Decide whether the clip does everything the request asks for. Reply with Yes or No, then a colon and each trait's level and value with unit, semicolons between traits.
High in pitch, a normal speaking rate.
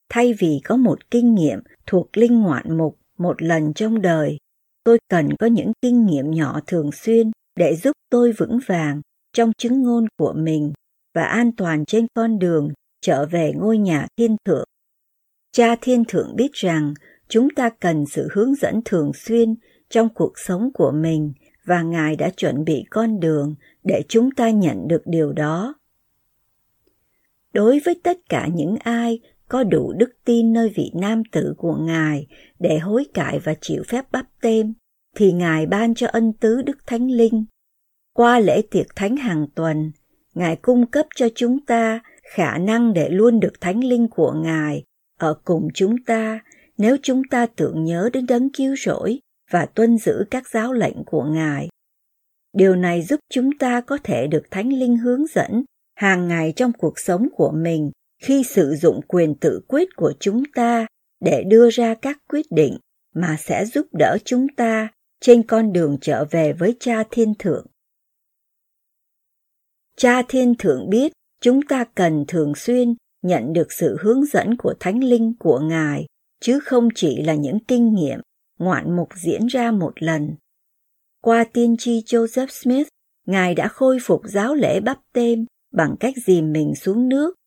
Yes: high, 225 Hz; average, 175 wpm